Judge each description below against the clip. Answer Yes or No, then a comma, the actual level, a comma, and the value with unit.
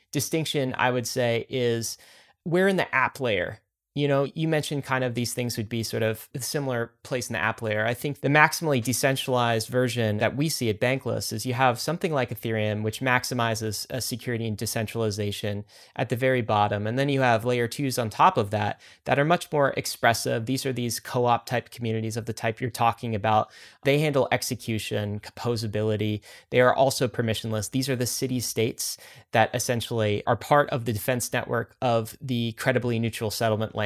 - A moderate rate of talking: Yes, average, 195 wpm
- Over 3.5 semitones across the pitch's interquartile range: No, average, 2.8 semitones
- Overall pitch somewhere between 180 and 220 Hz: No, low, 120 Hz